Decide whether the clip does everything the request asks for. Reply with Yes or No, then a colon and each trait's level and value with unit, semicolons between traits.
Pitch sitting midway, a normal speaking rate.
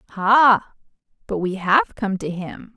No: high, 200 Hz; average, 150 wpm